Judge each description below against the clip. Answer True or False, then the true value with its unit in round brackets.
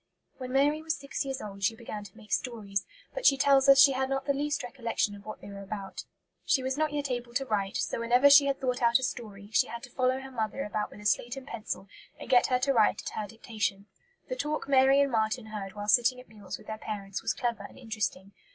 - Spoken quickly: True (250 wpm)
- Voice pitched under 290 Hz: True (240 Hz)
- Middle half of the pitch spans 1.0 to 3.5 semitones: False (4.2 semitones)